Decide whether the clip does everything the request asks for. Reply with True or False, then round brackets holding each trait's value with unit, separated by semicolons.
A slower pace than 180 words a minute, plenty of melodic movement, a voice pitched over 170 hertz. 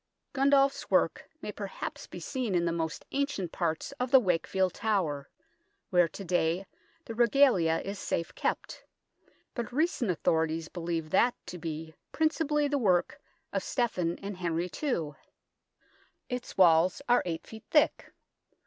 True (140 wpm; 7.1 semitones; 185 Hz)